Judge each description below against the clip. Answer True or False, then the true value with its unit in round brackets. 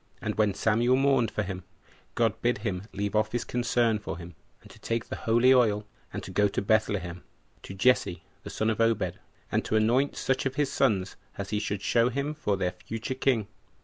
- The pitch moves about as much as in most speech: True (3.4 semitones)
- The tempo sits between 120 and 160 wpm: False (205 wpm)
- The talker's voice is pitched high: False (110 Hz)